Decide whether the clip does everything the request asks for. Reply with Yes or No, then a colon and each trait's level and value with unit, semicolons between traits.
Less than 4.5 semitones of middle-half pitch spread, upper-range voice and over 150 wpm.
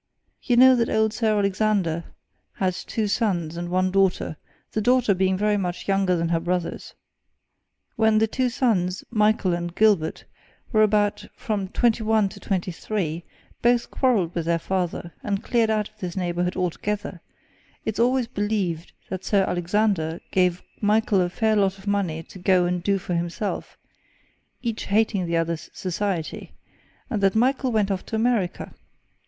Yes: average, 3.5 semitones; high, 195 Hz; average, 160 wpm